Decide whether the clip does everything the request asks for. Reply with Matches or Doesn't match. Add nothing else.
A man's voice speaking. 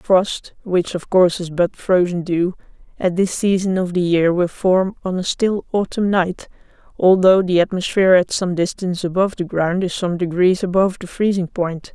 Doesn't match